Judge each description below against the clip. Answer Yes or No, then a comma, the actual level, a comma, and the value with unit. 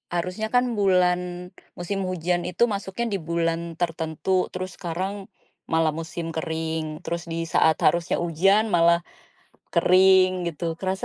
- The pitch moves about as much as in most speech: No, narrow, 2.3 semitones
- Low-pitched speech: No, medium, 175 Hz